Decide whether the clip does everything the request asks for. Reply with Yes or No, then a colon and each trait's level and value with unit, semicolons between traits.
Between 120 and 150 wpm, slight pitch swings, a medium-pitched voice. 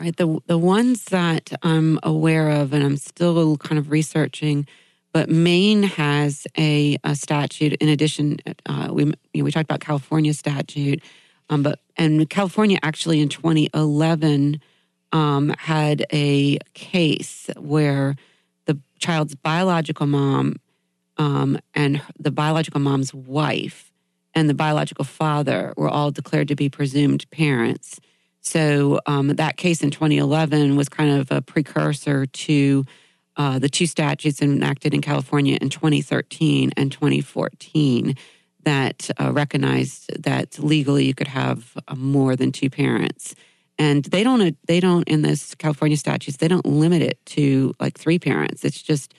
Yes: average, 145 wpm; narrow, 1.9 semitones; medium, 150 Hz